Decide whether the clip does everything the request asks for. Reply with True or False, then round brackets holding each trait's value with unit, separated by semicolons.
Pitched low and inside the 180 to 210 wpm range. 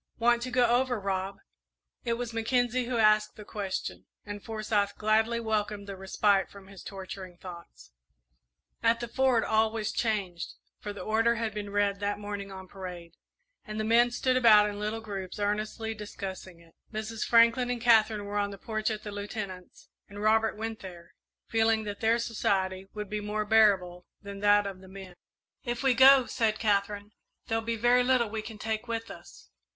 False (215 Hz; 185 wpm)